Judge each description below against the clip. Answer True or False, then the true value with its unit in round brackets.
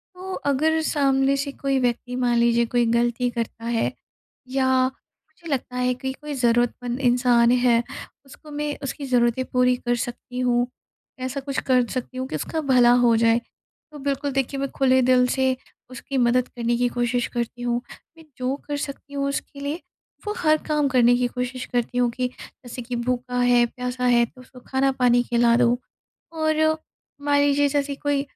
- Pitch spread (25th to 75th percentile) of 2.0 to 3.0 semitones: True (2.4 semitones)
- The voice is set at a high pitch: True (250 Hz)